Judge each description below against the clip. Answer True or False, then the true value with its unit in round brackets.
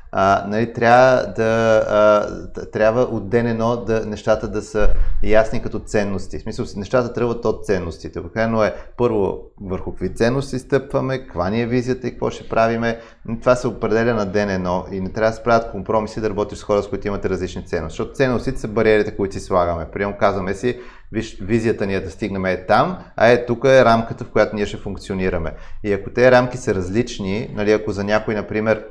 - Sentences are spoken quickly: True (210 wpm)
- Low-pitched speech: True (110 Hz)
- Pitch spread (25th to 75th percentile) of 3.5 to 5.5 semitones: False (2.7 semitones)